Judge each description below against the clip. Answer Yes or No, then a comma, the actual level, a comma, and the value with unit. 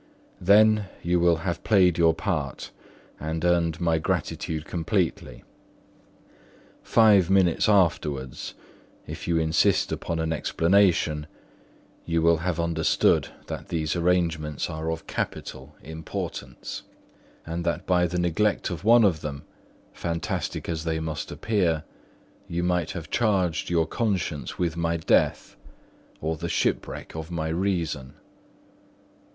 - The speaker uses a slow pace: Yes, slow, 125 wpm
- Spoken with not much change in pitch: Yes, narrow, 2.0 semitones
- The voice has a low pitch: Yes, very low, 85 Hz